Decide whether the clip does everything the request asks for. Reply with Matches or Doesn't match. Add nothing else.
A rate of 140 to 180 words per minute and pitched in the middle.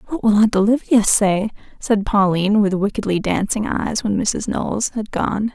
Doesn't match